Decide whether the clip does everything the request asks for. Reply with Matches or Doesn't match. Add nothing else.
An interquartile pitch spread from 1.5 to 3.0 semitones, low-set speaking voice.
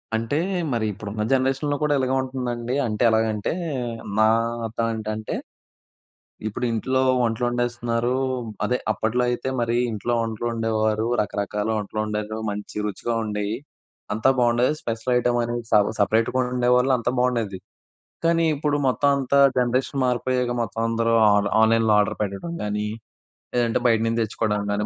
Matches